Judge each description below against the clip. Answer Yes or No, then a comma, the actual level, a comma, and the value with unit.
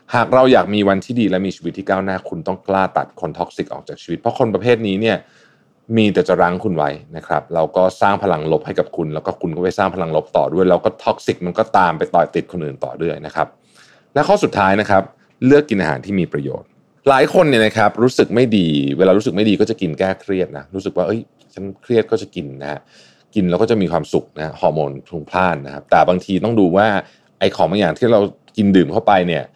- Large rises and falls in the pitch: No, average, 3.8 semitones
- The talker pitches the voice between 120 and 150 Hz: No, very low, 95 Hz